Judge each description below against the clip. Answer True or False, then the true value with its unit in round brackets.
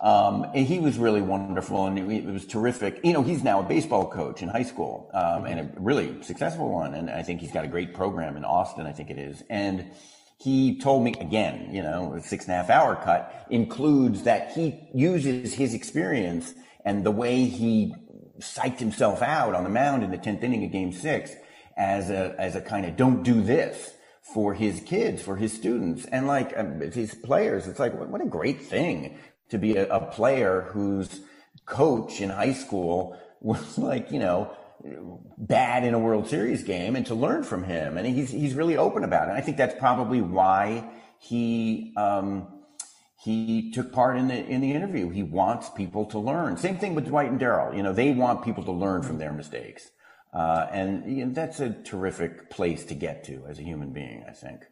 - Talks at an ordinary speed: False (210 wpm)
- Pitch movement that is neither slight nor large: True (5.0 semitones)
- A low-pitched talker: True (110 Hz)